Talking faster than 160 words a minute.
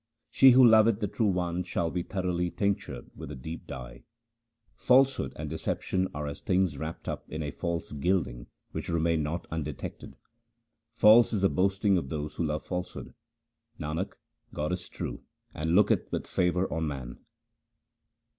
No: average, 155 wpm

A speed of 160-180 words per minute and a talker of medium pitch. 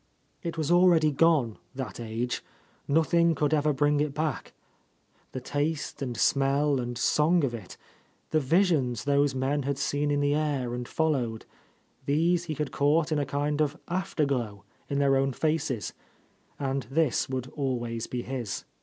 Yes: average, 170 wpm; medium, 145 Hz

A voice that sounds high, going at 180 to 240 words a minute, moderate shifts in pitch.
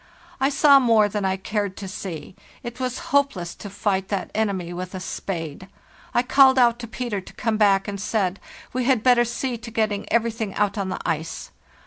Yes: high, 210 Hz; average, 200 wpm; average, 4.0 semitones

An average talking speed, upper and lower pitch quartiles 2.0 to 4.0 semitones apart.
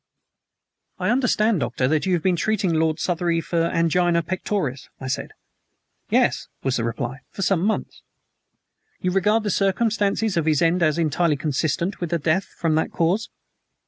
Yes: average, 165 wpm; average, 3.7 semitones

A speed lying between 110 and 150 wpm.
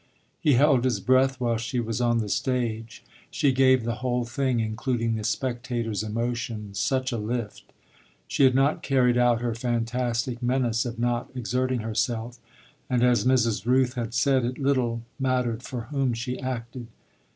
No: average, 160 wpm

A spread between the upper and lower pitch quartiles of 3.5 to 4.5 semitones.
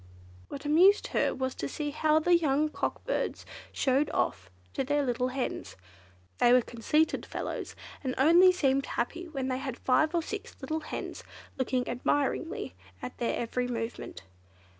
Yes: average, 3.8 semitones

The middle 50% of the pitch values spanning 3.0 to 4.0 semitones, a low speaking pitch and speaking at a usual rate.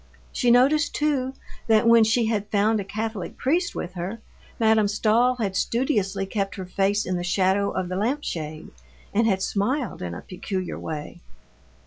No: average, 3.7 semitones; high, 210 Hz; average, 170 wpm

